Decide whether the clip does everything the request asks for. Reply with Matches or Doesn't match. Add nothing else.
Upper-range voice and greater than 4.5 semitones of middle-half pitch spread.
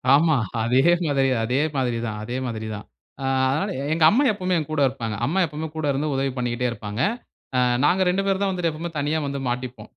Doesn't match